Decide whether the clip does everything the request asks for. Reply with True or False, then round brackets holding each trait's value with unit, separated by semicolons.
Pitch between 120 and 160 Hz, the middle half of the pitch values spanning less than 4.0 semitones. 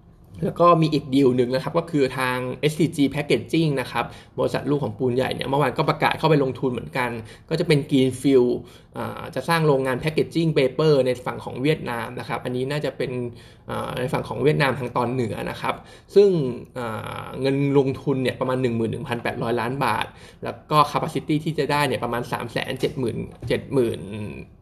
True (130 Hz; 3.3 semitones)